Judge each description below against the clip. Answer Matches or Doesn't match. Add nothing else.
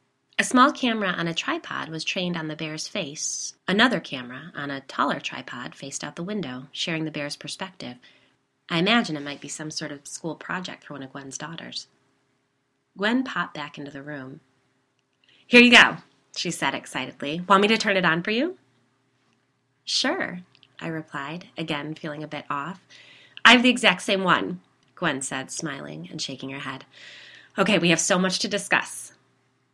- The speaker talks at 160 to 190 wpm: Matches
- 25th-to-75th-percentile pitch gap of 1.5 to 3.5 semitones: Doesn't match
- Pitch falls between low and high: Matches